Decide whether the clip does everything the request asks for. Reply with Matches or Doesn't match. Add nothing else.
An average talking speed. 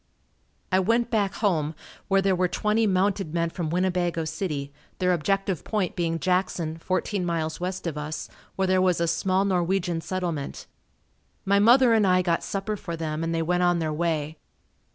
Matches